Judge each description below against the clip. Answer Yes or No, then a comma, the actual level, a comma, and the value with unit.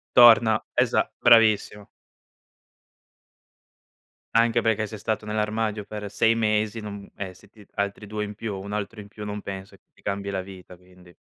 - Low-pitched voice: Yes, low, 105 Hz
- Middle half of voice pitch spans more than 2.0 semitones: No, narrow, 1.6 semitones